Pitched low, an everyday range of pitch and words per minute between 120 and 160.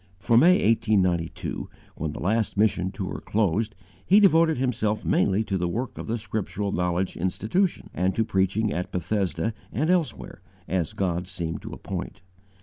Yes: low, 100 Hz; average, 3.9 semitones; average, 155 wpm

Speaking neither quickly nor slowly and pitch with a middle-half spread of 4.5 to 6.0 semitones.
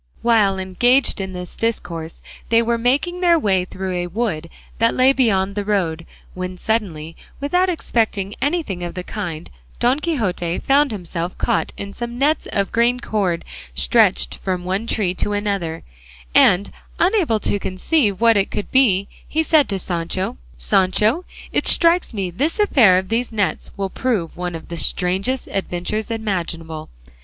Yes: average, 160 wpm; average, 5.1 semitones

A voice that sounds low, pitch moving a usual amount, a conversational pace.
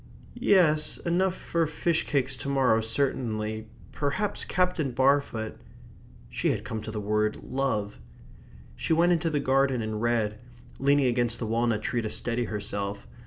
Yes: low, 125 Hz; average, 4.8 semitones; average, 155 wpm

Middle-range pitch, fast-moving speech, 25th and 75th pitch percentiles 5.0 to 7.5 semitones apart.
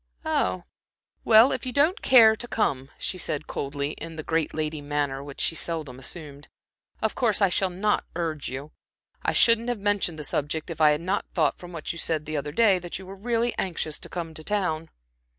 Yes: medium, 165 Hz; fast, 210 wpm; wide, 5.4 semitones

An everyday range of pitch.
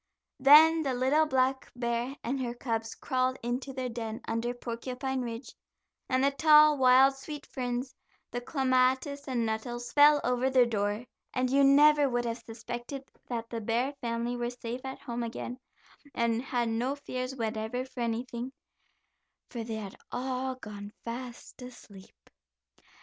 No: narrow, 2.2 semitones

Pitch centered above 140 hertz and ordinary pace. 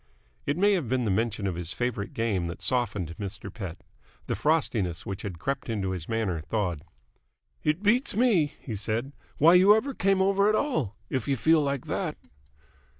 No: low, 120 Hz; average, 185 wpm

